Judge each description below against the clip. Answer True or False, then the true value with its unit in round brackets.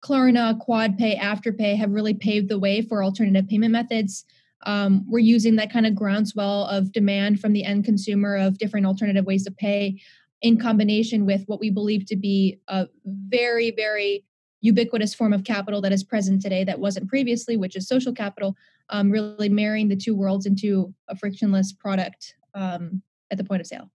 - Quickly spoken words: False (185 wpm)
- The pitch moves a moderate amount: False (1.8 semitones)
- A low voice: False (205 Hz)